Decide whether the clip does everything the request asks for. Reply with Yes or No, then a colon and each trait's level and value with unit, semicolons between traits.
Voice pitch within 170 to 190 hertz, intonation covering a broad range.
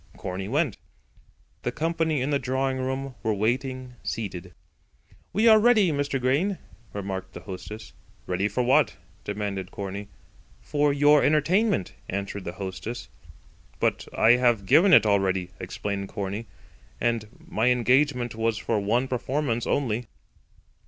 No: low, 120 Hz; wide, 5.8 semitones